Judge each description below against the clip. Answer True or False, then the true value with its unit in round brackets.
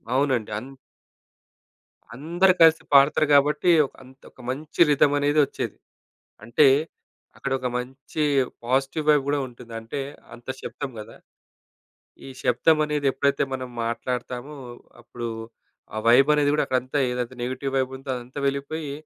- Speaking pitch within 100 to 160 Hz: True (135 Hz)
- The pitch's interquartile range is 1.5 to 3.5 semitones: True (2.8 semitones)